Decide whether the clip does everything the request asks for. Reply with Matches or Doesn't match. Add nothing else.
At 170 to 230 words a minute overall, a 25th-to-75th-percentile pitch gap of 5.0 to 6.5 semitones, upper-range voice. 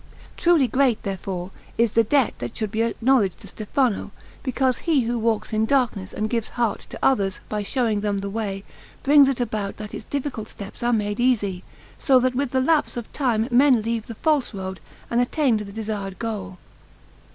Doesn't match